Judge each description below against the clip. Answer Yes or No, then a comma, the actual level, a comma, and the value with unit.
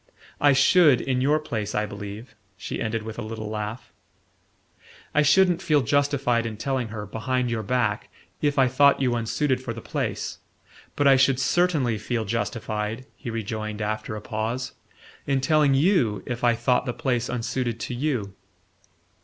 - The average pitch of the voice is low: Yes, low, 120 Hz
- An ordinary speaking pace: Yes, average, 165 wpm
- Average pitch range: Yes, average, 3.9 semitones